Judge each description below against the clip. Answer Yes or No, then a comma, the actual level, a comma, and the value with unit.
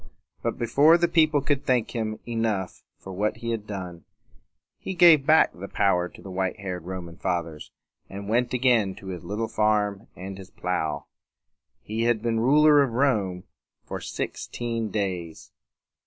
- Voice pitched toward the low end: Yes, low, 105 Hz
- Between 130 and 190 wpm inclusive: Yes, average, 165 wpm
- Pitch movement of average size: Yes, average, 4.5 semitones